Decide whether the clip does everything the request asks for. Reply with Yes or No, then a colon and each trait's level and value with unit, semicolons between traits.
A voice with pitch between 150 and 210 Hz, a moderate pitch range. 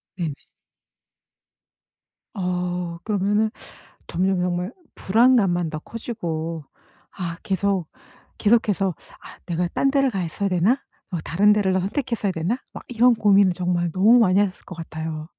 Yes: high, 190 Hz; average, 3.3 semitones